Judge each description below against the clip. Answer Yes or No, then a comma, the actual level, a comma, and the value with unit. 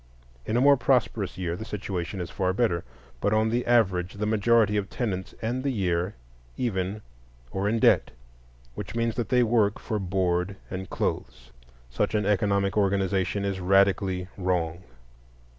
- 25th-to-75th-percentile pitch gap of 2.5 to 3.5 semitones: Yes, average, 2.9 semitones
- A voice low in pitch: Yes, low, 100 Hz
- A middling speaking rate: Yes, average, 160 wpm